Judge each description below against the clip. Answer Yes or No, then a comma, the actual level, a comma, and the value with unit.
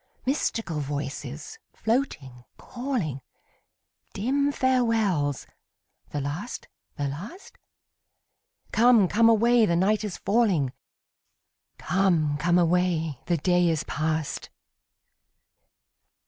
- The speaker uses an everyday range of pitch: No, wide, 7.4 semitones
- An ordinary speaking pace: No, slow, 90 wpm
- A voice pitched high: No, medium, 180 Hz